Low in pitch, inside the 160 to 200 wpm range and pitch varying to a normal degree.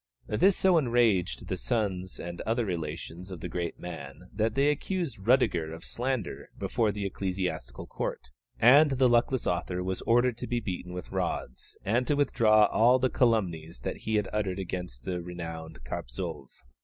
No: low, 100 Hz; average, 165 wpm; wide, 5.7 semitones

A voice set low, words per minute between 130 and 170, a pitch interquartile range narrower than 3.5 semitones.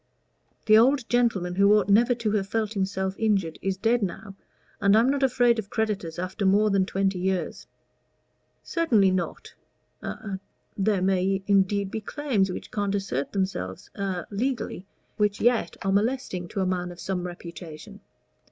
No: high, 200 Hz; average, 160 wpm; average, 2.8 semitones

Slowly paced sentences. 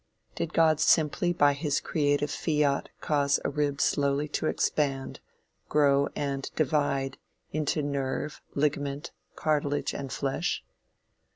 Yes: slow, 115 wpm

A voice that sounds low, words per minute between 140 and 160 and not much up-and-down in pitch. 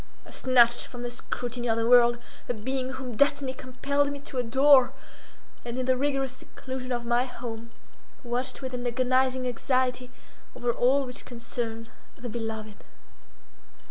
No: very high, 250 Hz; average, 150 wpm; narrow, 1.5 semitones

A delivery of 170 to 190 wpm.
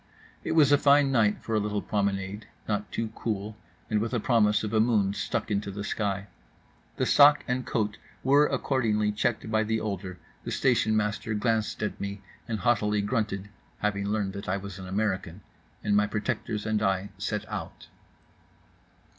Yes: average, 175 wpm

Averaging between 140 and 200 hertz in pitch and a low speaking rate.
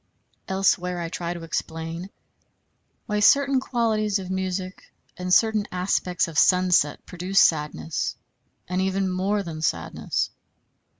Yes: medium, 185 Hz; slow, 120 wpm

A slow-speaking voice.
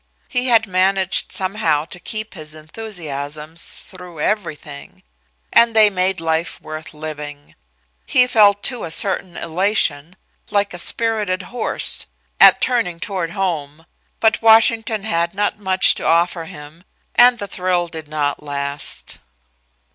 Yes: slow, 130 wpm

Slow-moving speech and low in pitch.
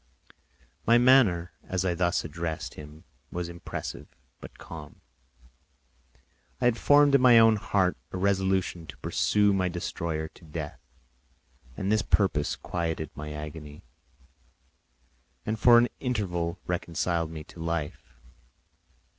Yes: slow, 125 wpm; very low, 90 Hz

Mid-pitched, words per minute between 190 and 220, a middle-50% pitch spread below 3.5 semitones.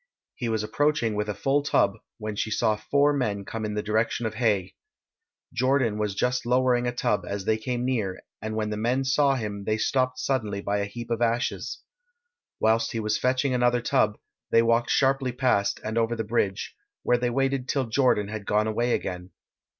No: low, 115 Hz; average, 195 wpm; average, 3.0 semitones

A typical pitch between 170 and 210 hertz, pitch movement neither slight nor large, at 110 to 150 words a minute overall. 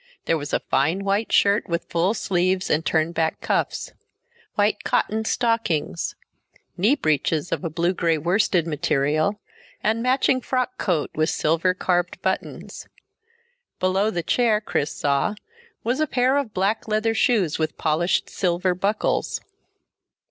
Yes: medium, 185 Hz; average, 5.0 semitones; average, 140 wpm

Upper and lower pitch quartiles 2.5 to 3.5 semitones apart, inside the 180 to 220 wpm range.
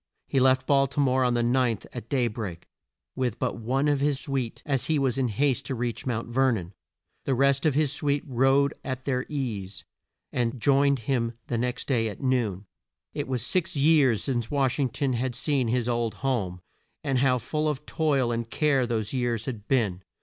Yes: average, 2.8 semitones; average, 200 wpm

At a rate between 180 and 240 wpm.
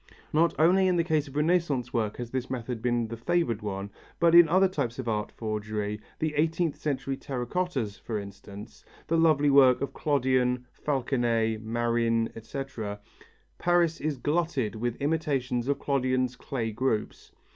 No: average, 155 wpm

